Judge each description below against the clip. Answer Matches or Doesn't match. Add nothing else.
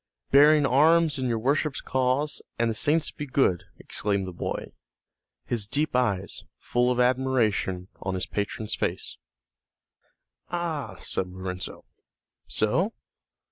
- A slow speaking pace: Matches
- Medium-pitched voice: Doesn't match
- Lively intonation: Matches